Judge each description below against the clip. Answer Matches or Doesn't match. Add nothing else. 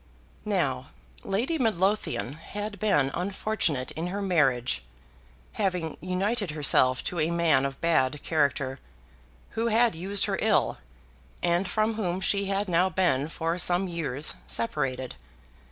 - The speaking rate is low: Matches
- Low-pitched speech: Doesn't match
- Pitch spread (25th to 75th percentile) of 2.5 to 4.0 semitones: Doesn't match